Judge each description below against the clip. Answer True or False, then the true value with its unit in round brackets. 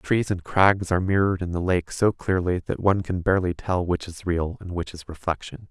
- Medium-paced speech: False (230 wpm)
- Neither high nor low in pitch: False (90 Hz)